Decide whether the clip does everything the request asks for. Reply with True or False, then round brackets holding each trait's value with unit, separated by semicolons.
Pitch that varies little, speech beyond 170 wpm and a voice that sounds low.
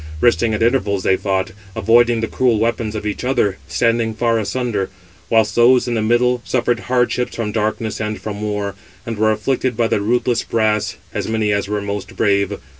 True (2.3 semitones; 190 wpm; 110 Hz)